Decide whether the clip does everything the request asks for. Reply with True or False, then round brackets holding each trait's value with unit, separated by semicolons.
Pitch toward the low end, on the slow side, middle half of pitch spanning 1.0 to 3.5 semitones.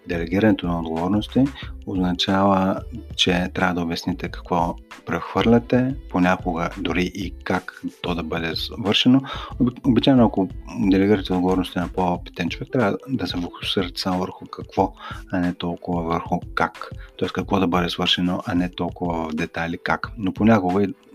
False (90 Hz; 145 wpm; 2.8 semitones)